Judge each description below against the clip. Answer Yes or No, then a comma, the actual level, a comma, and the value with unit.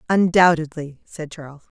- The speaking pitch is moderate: Yes, medium, 160 Hz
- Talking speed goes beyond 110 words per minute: No, slow, 100 wpm